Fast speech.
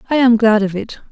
Yes: fast, 270 wpm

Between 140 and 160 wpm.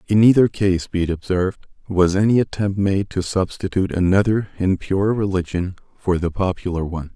No: average, 170 wpm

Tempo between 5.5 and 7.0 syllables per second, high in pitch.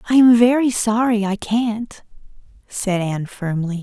No: 4.4 syllables/s; high, 215 Hz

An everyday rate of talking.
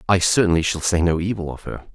No: fast, 245 wpm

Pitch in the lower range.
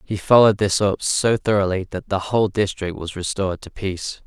Yes: low, 100 Hz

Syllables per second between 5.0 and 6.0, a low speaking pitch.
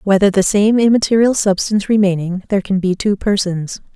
No: 5.7 syllables/s; high, 200 Hz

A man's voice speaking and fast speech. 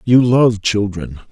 No: male; slow, 135 wpm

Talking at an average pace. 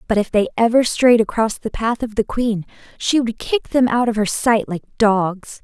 No: fast, 225 wpm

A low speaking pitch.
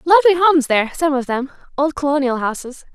No: very high, 290 Hz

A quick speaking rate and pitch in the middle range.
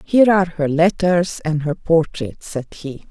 No: average, 175 wpm; medium, 165 Hz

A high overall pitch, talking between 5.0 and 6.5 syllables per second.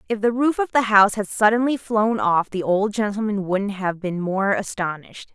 Yes: high, 205 Hz; 5.1 syllables/s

